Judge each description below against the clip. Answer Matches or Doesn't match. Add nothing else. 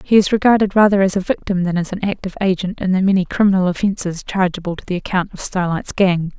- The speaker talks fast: Matches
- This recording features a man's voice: Doesn't match